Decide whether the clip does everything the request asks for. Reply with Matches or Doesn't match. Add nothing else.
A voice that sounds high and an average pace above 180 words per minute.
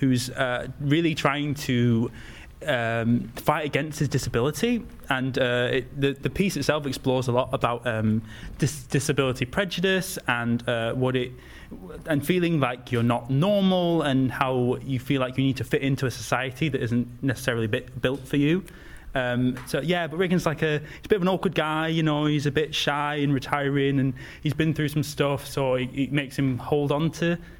Doesn't match